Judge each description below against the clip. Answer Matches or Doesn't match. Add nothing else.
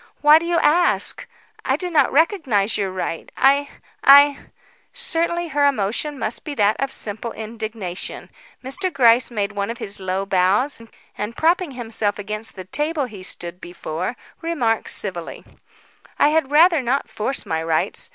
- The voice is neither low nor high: Doesn't match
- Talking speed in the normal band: Matches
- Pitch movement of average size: Doesn't match